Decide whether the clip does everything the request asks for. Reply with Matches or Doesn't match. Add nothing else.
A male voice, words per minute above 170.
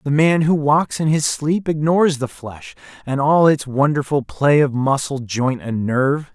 Matches